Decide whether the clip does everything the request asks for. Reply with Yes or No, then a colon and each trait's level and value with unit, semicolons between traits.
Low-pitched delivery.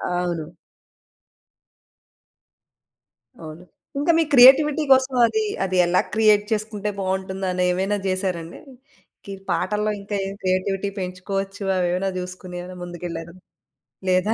No: high, 190 Hz